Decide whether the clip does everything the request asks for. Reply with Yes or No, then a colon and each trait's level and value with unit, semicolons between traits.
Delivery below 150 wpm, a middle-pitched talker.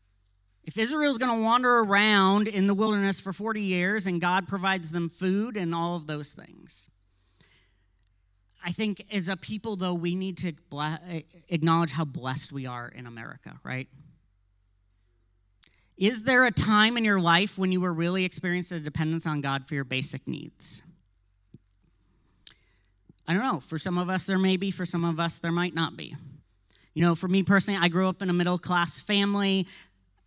No: average, 180 wpm; medium, 170 Hz